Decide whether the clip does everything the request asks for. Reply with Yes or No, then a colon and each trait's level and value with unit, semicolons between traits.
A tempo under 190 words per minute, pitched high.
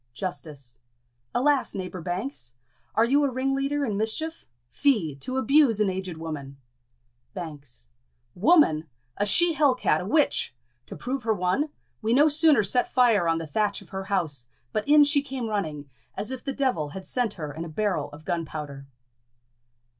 Yes: average, 170 wpm; high, 205 Hz